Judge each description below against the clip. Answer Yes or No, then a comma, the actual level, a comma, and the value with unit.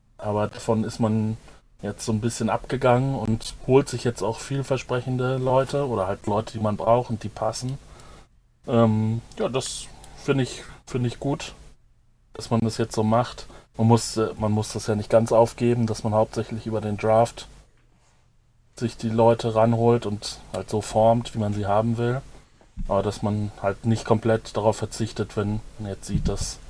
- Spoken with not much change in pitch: Yes, narrow, 2.0 semitones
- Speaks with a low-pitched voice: Yes, low, 115 Hz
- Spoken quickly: No, average, 180 wpm